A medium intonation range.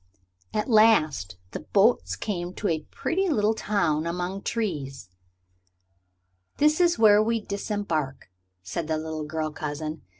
No: wide, 5.8 semitones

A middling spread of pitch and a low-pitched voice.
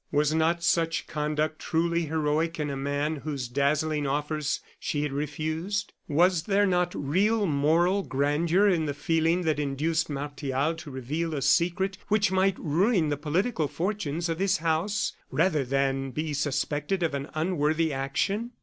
No: average, 3.2 semitones; medium, 155 Hz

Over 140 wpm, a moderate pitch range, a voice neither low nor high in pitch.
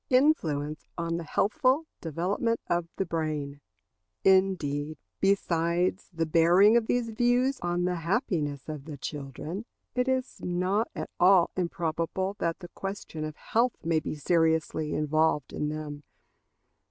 No: slow, 135 wpm; average, 4.3 semitones; medium, 170 Hz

